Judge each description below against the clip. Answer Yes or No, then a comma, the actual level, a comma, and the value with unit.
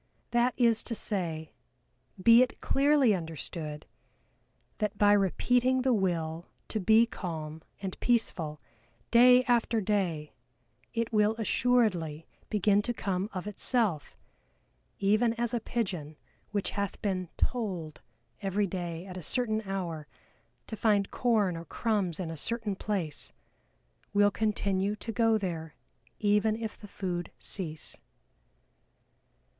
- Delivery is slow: Yes, slow, 125 wpm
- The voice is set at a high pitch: Yes, high, 205 Hz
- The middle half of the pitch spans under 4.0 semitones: No, average, 4.6 semitones